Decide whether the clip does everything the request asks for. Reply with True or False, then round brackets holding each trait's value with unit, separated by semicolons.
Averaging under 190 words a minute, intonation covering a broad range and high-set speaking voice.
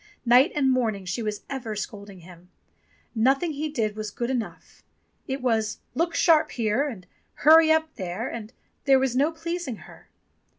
True (175 wpm; 5.8 semitones; 250 Hz)